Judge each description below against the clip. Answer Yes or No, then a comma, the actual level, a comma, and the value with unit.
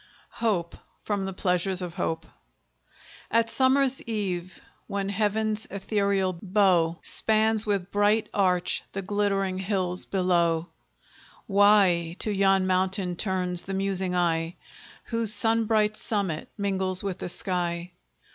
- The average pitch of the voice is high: Yes, high, 195 Hz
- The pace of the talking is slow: Yes, slow, 120 wpm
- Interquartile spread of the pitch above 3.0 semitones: No, narrow, 2.5 semitones